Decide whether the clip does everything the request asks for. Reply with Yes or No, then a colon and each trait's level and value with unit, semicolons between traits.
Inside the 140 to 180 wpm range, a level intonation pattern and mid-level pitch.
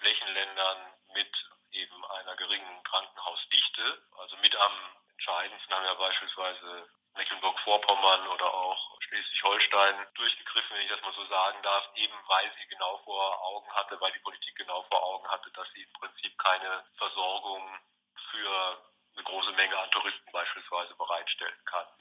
No: average, 145 wpm; narrow, 1.1 semitones; very low, 95 Hz